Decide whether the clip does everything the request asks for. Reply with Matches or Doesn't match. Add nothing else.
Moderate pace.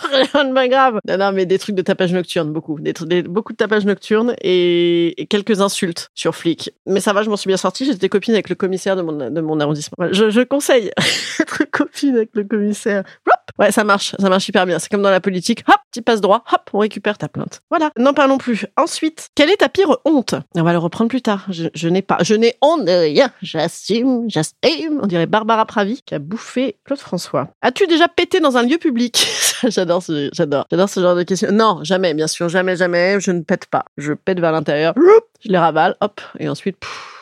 Doesn't match